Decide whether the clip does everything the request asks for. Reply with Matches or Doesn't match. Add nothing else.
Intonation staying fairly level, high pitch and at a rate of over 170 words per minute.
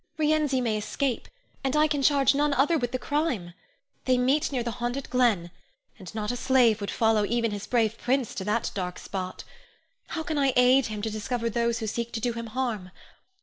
Doesn't match